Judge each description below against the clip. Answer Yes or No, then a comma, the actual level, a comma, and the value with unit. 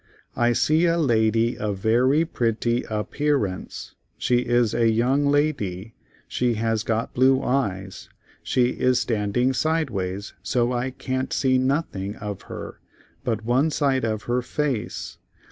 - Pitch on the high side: No, low, 120 Hz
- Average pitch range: Yes, average, 3.3 semitones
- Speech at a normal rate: Yes, average, 165 wpm